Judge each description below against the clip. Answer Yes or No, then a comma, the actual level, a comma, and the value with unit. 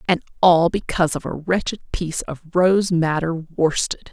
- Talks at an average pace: Yes, average, 160 wpm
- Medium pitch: Yes, medium, 170 Hz